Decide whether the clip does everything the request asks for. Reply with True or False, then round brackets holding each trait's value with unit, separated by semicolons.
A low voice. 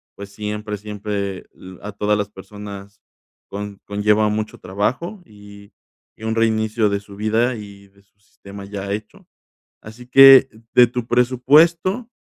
True (105 Hz)